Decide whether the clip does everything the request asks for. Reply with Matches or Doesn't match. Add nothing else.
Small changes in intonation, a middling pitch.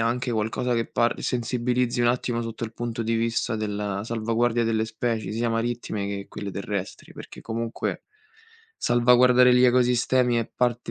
Doesn't match